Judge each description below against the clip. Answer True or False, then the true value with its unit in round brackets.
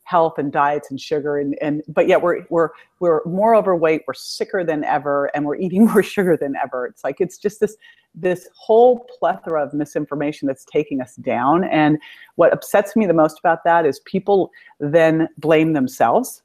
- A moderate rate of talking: True (190 wpm)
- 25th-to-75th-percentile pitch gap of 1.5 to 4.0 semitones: False (4.6 semitones)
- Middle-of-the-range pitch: True (160 Hz)